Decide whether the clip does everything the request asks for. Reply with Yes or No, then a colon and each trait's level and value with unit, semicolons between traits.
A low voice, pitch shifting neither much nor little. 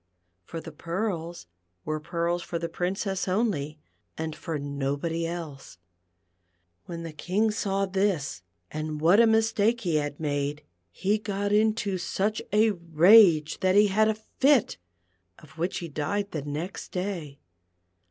No: medium, 175 Hz; average, 4.9 semitones